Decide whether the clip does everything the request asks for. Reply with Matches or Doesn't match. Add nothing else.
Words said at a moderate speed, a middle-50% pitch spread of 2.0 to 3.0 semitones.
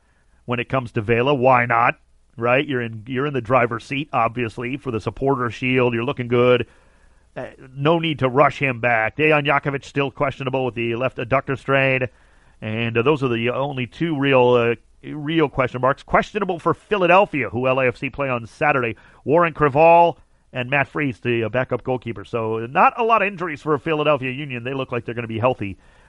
Doesn't match